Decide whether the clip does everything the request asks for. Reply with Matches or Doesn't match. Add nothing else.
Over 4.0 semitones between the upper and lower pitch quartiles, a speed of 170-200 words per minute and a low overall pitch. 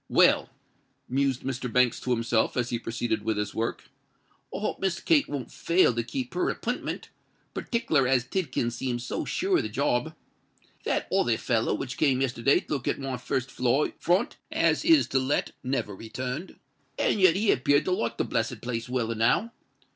Matches